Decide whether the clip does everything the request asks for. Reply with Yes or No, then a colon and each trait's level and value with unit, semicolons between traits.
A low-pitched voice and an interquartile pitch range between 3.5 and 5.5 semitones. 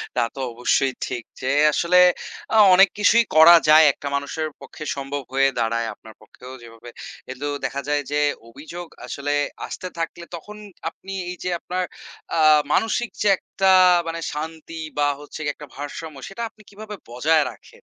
No: medium, 155 Hz; average, 4.3 semitones